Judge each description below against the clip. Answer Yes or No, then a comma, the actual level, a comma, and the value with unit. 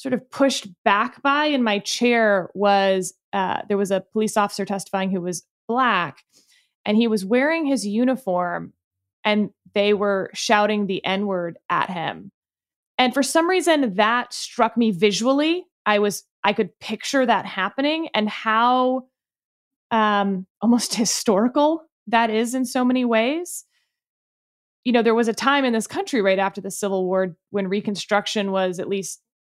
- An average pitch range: Yes, average, 4.4 semitones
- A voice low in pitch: No, high, 220 Hz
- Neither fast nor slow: Yes, average, 160 wpm